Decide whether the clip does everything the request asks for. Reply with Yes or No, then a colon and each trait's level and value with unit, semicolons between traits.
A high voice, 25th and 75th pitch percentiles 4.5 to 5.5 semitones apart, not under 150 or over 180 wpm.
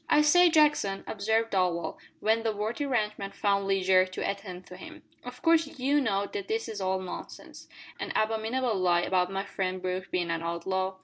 No: high, 200 Hz; average, 5.0 semitones; average, 190 wpm